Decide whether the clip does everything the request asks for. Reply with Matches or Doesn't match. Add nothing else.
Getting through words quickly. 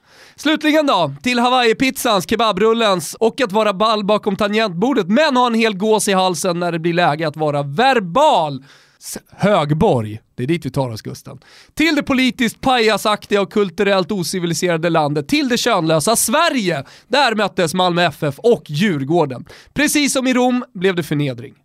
Doesn't match